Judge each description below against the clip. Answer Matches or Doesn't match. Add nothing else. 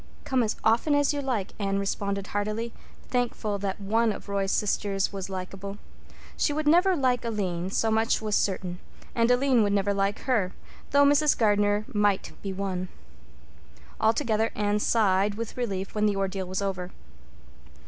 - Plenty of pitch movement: Doesn't match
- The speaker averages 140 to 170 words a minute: Matches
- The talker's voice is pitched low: Doesn't match